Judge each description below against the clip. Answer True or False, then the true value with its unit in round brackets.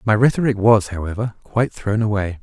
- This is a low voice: True (110 Hz)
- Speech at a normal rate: True (175 wpm)